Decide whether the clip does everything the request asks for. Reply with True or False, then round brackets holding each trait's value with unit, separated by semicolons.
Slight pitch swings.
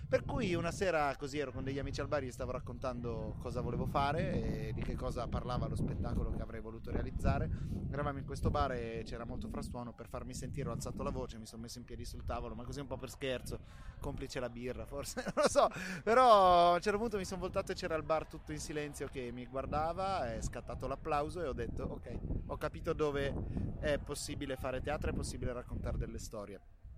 False (4.1 semitones)